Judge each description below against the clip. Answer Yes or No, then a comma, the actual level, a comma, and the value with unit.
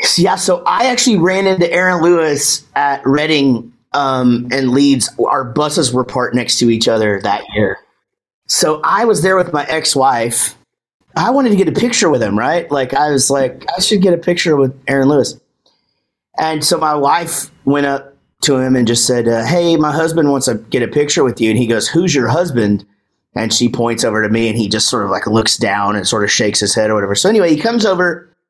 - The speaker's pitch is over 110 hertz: Yes, medium, 140 Hz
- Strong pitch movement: Yes, wide, 6.3 semitones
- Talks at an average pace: No, fast, 225 wpm